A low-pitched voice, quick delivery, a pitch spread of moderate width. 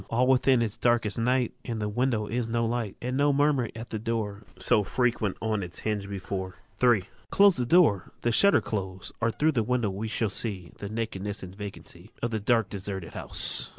Yes: low, 110 Hz; fast, 210 wpm; average, 3.3 semitones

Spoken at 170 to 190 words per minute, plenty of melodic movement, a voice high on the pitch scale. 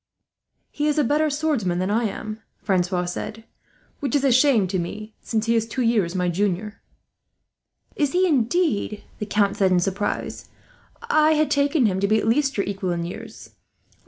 Yes: average, 185 wpm; wide, 6.6 semitones; high, 220 Hz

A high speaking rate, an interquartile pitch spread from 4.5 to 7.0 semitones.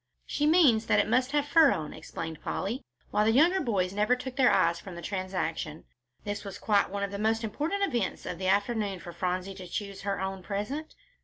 Yes: fast, 215 wpm; average, 5.1 semitones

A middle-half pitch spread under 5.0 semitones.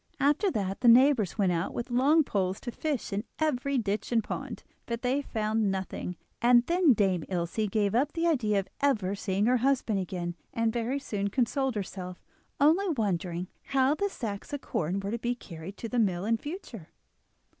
No: wide, 5.6 semitones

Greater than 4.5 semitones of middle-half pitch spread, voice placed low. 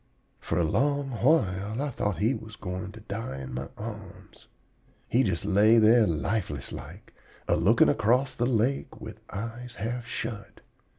No: average, 3.7 semitones; low, 110 Hz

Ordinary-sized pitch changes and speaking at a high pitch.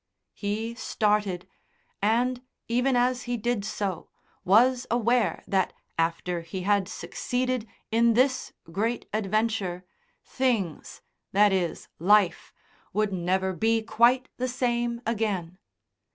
Yes: average, 4.2 semitones; high, 215 Hz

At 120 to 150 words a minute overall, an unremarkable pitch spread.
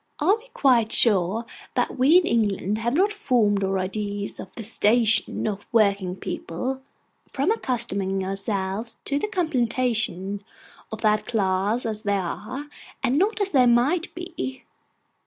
Yes: average, 145 wpm; average, 4.9 semitones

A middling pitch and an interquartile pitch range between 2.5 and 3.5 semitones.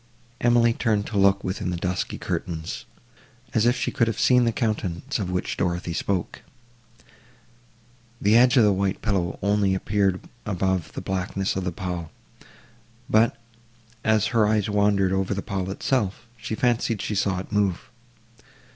No: low, 100 Hz; average, 2.9 semitones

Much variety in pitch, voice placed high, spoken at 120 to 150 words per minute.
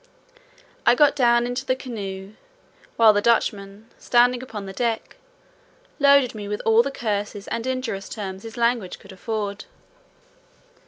No: average, 3.3 semitones; high, 225 Hz; average, 145 wpm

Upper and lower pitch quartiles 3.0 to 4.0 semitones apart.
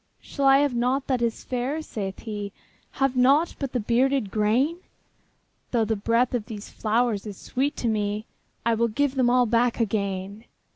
Yes: average, 3.4 semitones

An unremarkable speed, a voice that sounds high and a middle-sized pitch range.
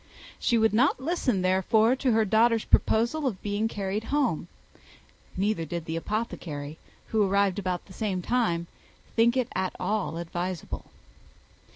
Yes: average, 145 wpm; high, 210 Hz; average, 4.0 semitones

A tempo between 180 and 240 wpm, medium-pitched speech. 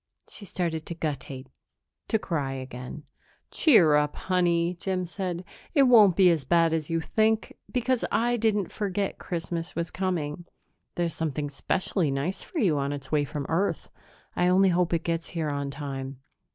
No: average, 165 wpm; medium, 170 Hz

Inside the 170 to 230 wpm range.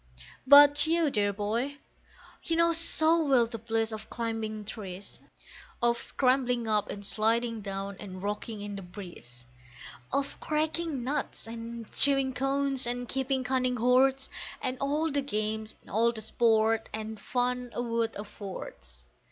No: average, 145 wpm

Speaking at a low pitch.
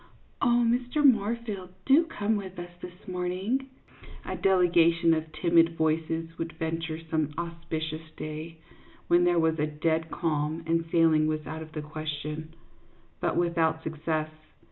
No: medium, 165 Hz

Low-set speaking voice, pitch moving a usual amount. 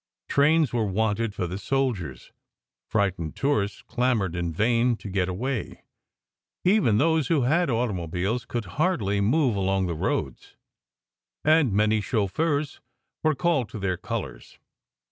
No: low, 110 Hz; wide, 6.1 semitones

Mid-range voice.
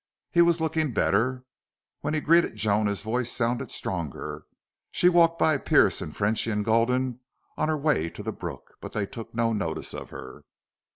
No: low, 120 Hz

